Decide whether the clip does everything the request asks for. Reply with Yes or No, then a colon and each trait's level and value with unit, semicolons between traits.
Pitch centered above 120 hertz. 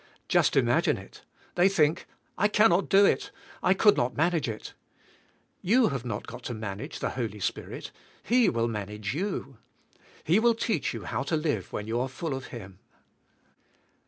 Yes: medium, 140 Hz